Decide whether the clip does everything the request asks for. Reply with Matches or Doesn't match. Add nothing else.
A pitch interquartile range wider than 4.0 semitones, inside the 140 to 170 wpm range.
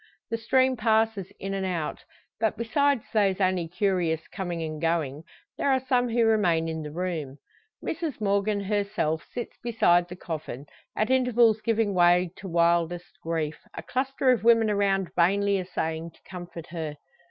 Matches